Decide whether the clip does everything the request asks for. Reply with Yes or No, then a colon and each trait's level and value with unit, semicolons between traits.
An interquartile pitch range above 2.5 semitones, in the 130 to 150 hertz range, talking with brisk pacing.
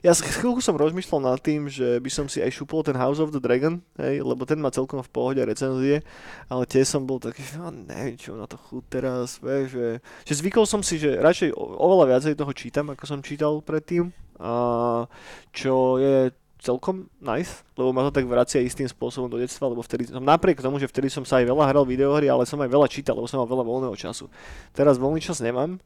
Yes: average, 2.9 semitones; low, 135 Hz; fast, 220 wpm